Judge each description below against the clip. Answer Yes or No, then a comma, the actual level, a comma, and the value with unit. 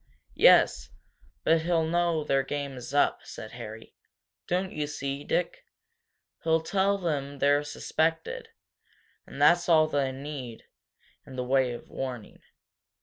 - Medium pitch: Yes, medium, 145 Hz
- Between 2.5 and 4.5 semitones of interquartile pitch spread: Yes, average, 3.6 semitones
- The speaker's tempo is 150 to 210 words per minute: No, slow, 135 wpm